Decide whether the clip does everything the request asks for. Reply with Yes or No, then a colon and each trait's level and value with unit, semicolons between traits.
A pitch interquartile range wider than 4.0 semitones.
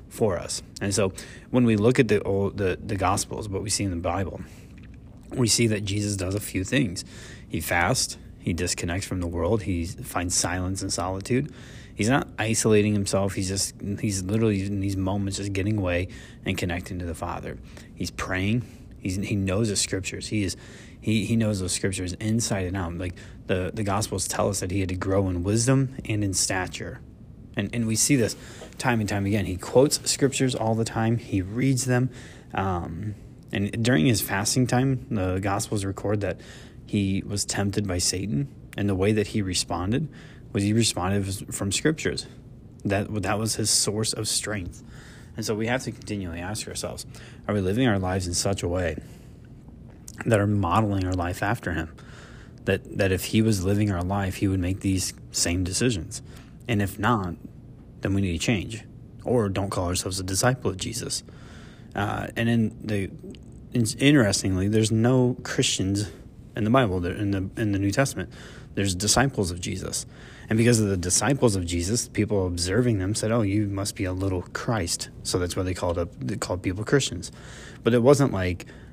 No: average, 3.5 semitones